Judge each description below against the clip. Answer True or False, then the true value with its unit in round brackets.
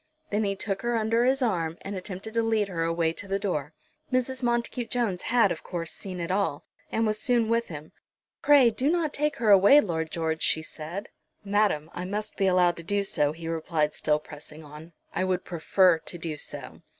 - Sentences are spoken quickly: True (210 wpm)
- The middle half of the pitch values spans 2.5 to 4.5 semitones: False (5.4 semitones)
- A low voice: False (190 Hz)